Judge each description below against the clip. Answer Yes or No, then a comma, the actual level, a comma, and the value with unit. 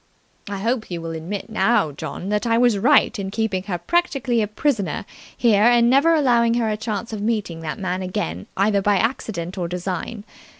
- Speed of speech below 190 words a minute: No, average, 195 wpm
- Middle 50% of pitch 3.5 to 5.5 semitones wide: Yes, average, 4.1 semitones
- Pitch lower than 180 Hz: No, high, 210 Hz